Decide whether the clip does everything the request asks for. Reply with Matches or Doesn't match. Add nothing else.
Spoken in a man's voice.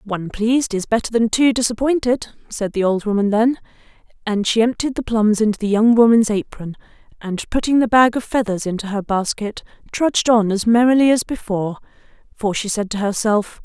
Doesn't match